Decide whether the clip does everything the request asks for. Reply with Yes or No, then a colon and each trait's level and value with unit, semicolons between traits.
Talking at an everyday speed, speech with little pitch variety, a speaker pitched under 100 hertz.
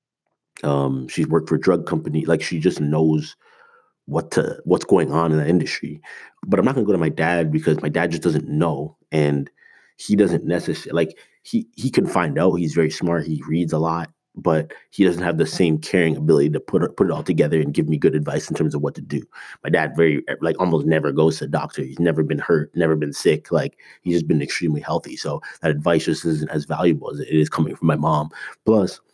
No: fast, 235 wpm; narrow, 1.4 semitones; very low, 80 Hz